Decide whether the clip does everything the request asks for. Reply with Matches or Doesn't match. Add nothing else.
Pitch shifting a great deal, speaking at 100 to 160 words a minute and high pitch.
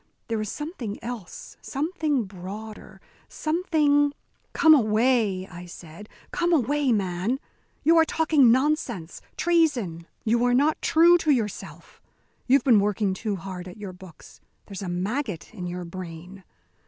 Matches